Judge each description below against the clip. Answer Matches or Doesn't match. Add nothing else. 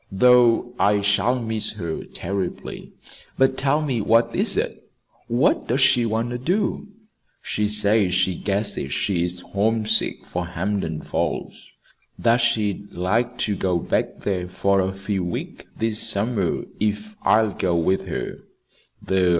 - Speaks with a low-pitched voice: Matches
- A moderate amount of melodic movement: Matches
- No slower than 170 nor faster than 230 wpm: Doesn't match